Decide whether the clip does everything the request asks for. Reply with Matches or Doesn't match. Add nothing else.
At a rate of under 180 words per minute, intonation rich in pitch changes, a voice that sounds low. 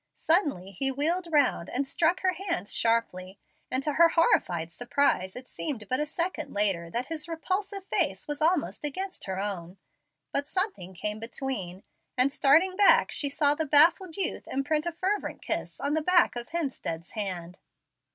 Doesn't match